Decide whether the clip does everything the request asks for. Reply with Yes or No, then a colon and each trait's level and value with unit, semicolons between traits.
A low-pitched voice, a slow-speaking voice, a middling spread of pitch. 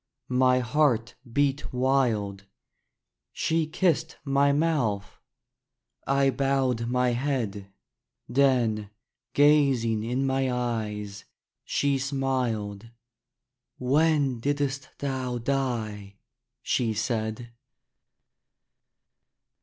Yes: low, 130 Hz; slow, 75 wpm; average, 3.6 semitones